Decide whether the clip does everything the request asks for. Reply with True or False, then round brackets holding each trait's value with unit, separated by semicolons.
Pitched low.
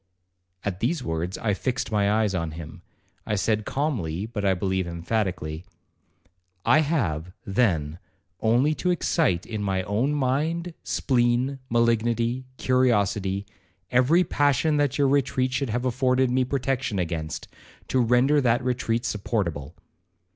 True (115 Hz)